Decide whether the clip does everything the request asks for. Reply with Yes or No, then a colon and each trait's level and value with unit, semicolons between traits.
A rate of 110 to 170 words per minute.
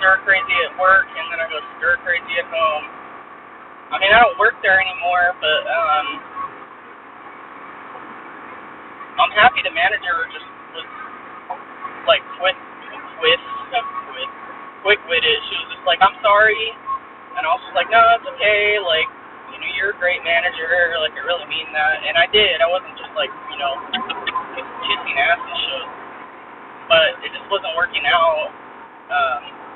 Yes: average, 160 wpm